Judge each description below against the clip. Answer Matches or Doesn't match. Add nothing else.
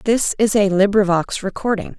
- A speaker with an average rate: Matches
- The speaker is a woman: Matches